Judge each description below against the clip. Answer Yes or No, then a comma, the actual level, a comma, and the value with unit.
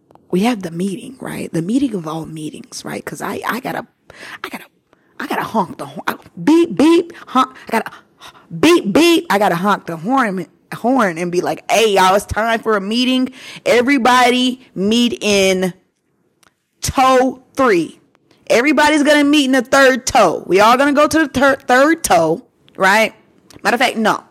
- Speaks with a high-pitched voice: Yes, very high, 250 Hz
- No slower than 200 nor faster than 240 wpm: No, average, 180 wpm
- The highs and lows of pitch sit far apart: Yes, wide, 6.3 semitones